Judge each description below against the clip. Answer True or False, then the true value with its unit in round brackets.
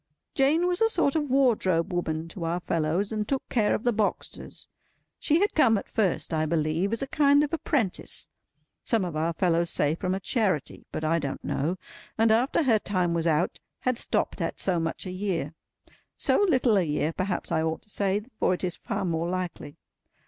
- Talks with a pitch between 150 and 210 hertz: True (185 Hz)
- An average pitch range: False (6.2 semitones)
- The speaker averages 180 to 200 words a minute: True (195 wpm)